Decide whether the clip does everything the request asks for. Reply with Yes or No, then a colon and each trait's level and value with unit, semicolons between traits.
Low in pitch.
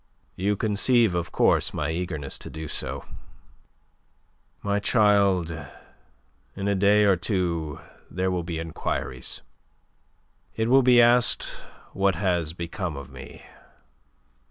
Yes: very low, 95 Hz